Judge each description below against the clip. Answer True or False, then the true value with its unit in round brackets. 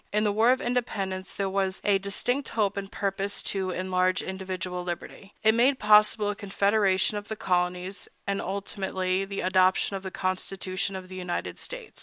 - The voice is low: False (195 Hz)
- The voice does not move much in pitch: True (1.8 semitones)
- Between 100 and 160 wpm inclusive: False (175 wpm)